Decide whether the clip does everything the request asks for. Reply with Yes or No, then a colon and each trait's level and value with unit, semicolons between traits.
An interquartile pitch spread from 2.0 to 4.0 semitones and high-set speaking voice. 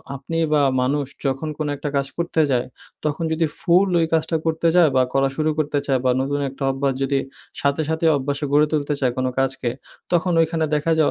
No: average, 2.8 semitones; medium, 145 Hz